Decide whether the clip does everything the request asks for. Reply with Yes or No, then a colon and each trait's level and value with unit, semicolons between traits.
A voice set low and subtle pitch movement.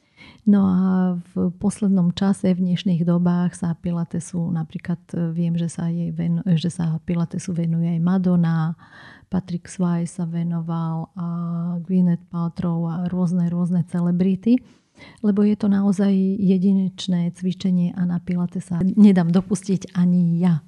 No: medium, 175 Hz; narrow, 1.6 semitones